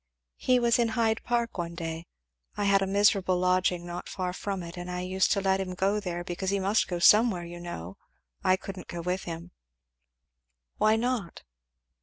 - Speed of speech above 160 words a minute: Yes, average, 200 wpm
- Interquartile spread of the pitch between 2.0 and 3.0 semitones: Yes, average, 2.7 semitones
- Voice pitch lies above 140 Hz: Yes, medium, 185 Hz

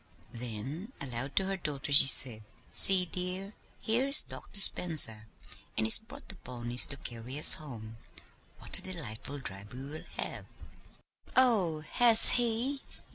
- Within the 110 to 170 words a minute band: Yes, average, 140 wpm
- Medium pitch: Yes, medium, 150 Hz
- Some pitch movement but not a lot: No, wide, 8.4 semitones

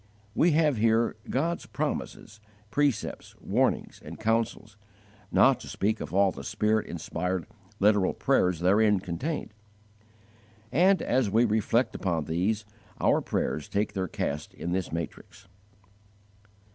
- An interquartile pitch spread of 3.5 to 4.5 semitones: Yes, average, 4.2 semitones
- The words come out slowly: Yes, slow, 125 wpm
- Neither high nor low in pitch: No, low, 105 Hz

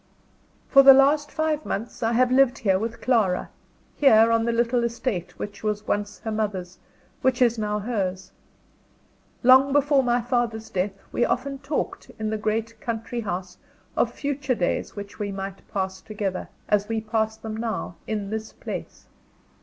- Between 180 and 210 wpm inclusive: No, average, 165 wpm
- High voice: Yes, high, 225 Hz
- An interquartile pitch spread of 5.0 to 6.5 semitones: No, average, 3.3 semitones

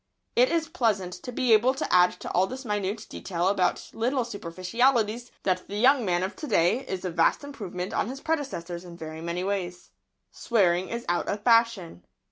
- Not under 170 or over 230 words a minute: Yes, average, 190 wpm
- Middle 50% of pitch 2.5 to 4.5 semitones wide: No, average, 5.2 semitones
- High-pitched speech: Yes, high, 200 Hz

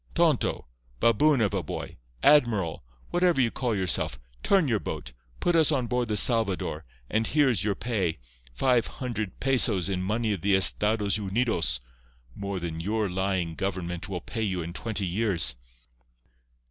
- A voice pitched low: Yes, low, 100 Hz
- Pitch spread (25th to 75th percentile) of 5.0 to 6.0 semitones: Yes, wide, 5.5 semitones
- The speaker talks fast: No, average, 145 wpm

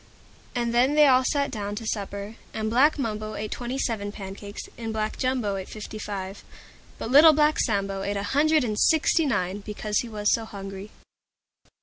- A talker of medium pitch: No, high, 215 Hz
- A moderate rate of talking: Yes, average, 185 wpm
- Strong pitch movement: No, average, 4.0 semitones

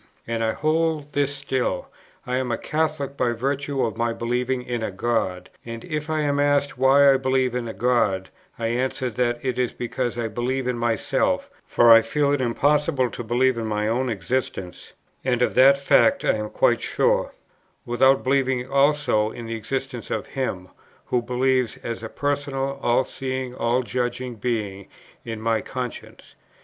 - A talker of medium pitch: No, low, 125 Hz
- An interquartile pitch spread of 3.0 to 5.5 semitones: No, narrow, 2.6 semitones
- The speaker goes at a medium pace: Yes, average, 175 wpm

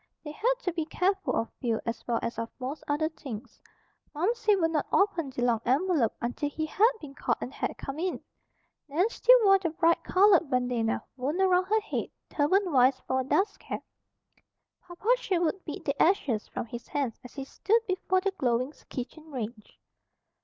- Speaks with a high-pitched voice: Yes, very high, 310 Hz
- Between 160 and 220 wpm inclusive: Yes, average, 185 wpm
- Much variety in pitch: Yes, wide, 6.7 semitones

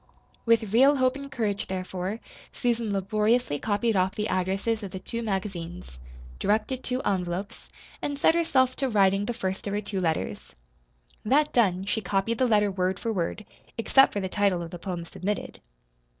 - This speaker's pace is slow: No, average, 175 wpm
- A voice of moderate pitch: No, high, 205 Hz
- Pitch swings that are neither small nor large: Yes, average, 3.7 semitones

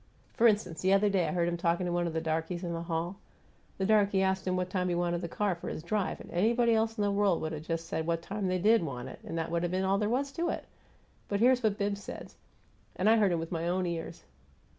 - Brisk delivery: Yes, fast, 280 wpm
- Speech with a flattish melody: No, average, 3.3 semitones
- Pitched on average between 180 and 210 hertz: Yes, medium, 185 Hz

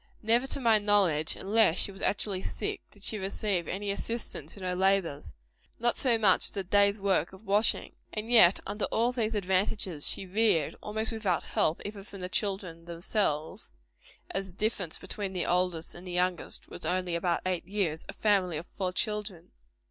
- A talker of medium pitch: No, high, 195 Hz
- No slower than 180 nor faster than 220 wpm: Yes, average, 185 wpm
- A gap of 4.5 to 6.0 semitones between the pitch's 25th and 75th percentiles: No, average, 2.9 semitones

